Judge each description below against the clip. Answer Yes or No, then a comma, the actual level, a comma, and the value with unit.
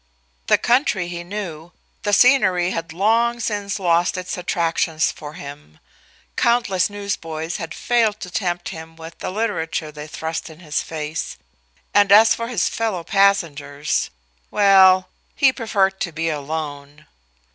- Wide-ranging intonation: No, average, 4.1 semitones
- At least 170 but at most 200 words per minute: No, average, 140 wpm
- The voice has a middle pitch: Yes, medium, 180 Hz